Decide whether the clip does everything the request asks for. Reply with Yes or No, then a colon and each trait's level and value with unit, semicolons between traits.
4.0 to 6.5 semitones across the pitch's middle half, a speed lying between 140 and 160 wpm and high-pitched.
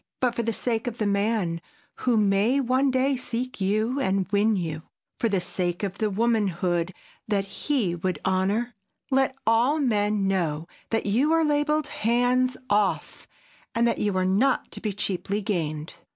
Yes: average, 4.3 semitones; average, 155 wpm; high, 215 Hz